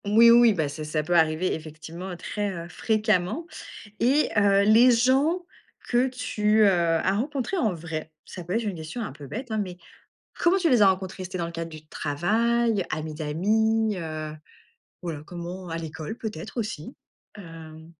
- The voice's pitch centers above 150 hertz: Yes, medium, 185 Hz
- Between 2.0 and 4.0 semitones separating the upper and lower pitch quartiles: No, wide, 5.5 semitones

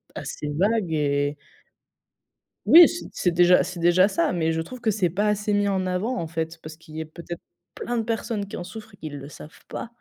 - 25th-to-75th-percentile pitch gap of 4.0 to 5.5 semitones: Yes, average, 4.5 semitones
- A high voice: No, medium, 180 Hz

